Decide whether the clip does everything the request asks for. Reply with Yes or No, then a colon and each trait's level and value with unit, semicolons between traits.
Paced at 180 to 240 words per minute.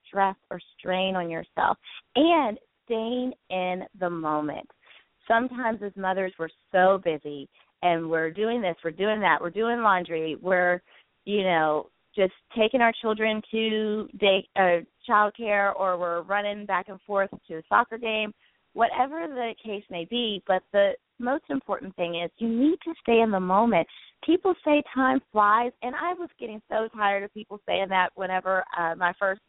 No: average, 170 wpm